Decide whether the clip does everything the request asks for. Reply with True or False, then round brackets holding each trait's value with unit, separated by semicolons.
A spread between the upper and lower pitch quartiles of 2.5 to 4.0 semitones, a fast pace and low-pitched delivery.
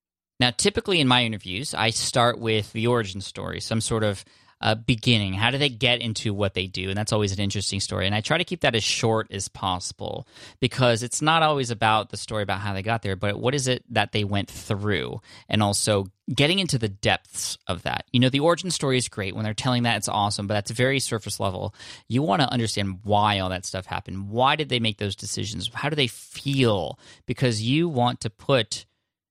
True (3.7 semitones; 225 wpm; 110 Hz)